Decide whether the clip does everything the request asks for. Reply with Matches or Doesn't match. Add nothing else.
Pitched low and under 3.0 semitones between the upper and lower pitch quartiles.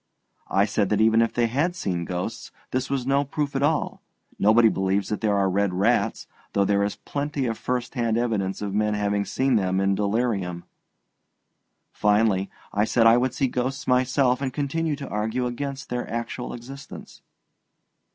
Doesn't match